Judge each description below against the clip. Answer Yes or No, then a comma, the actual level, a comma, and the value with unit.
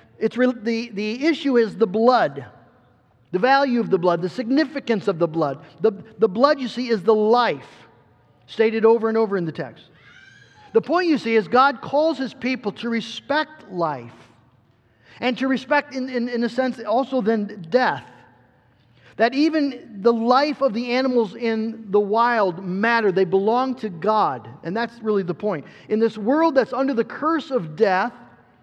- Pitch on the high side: Yes, high, 225 Hz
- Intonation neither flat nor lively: No, wide, 6.3 semitones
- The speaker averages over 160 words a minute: Yes, average, 180 wpm